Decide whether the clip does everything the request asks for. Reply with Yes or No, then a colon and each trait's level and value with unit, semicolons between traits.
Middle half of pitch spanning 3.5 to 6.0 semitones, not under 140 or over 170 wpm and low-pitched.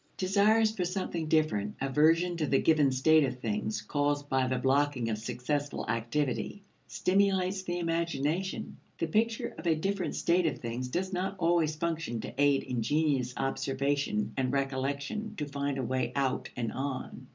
No: average, 4.8 semitones; average, 160 wpm; medium, 145 Hz